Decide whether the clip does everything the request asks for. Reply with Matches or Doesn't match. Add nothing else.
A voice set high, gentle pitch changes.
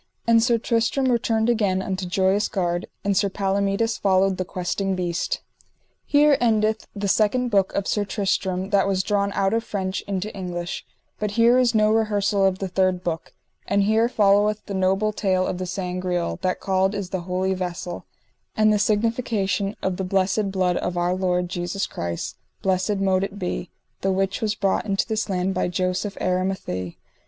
Matches